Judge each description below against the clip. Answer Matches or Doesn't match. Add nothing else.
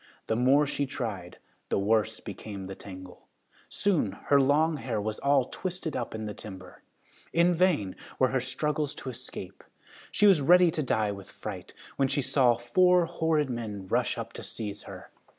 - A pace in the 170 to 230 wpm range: Matches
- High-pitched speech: Doesn't match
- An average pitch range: Doesn't match